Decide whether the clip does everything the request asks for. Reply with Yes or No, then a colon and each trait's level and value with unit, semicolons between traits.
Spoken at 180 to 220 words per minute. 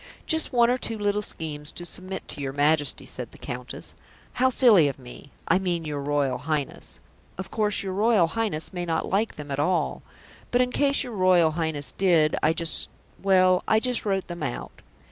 Yes: average, 195 wpm